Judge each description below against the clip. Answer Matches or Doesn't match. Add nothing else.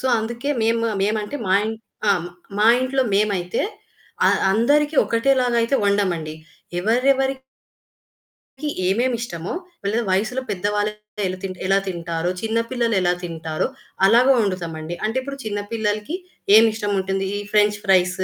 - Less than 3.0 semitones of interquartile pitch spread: Doesn't match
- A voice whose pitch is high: Matches